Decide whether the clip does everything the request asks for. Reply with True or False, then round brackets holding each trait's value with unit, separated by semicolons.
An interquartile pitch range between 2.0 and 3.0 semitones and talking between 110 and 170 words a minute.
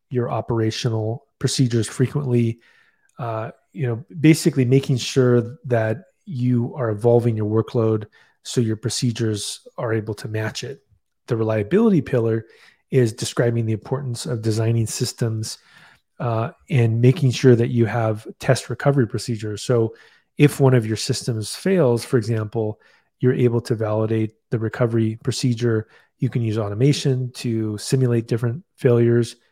True (2.7 semitones; 140 wpm)